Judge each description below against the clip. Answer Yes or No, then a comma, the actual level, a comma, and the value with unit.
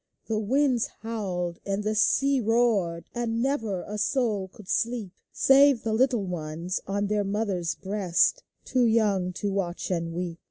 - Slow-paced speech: No, average, 155 wpm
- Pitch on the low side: No, high, 210 Hz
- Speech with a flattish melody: No, average, 4.2 semitones